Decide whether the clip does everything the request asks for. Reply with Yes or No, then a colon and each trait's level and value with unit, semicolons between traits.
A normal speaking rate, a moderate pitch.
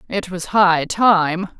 Yes: average, 150 wpm; medium, 180 Hz